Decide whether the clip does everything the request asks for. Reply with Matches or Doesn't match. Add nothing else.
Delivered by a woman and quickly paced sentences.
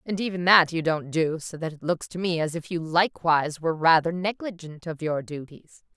Matches